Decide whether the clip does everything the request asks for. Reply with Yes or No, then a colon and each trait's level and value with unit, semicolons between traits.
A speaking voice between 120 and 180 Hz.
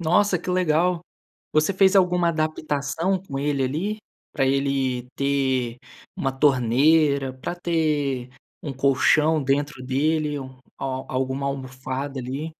Yes: medium, 140 Hz